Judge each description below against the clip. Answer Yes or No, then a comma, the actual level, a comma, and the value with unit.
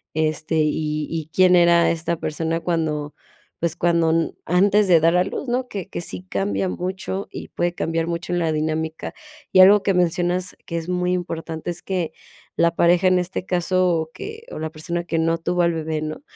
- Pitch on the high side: No, medium, 170 Hz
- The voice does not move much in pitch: Yes, narrow, 2.1 semitones